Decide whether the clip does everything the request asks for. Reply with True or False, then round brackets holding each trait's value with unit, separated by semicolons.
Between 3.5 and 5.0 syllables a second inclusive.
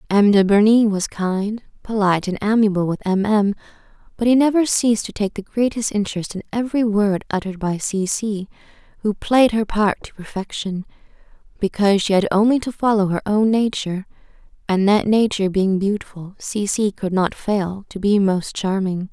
False (5.2 syllables/s)